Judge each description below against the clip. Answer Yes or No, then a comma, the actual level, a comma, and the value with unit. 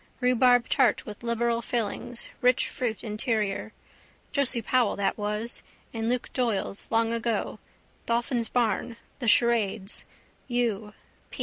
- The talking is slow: Yes, slow, 115 wpm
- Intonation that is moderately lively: No, narrow, 2.1 semitones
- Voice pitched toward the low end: No, high, 235 Hz